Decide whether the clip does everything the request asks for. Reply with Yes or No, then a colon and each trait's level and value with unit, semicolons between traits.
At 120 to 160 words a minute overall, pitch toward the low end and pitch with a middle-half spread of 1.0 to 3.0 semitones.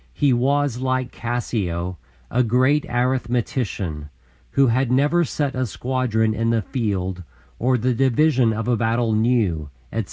Yes: average, 140 wpm; low, 120 Hz; average, 2.7 semitones